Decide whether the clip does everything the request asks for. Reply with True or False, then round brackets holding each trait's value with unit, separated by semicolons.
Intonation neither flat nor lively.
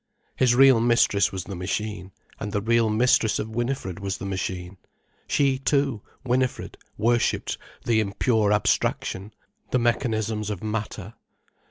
True (3.3 semitones)